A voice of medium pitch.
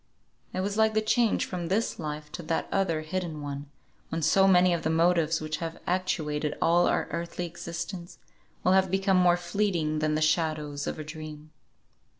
Yes: medium, 170 Hz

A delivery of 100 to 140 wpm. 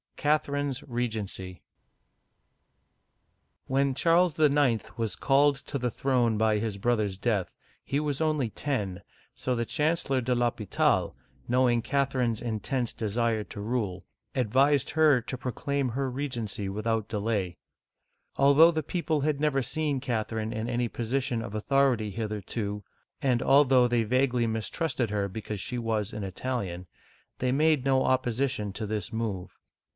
Yes: slow, 135 wpm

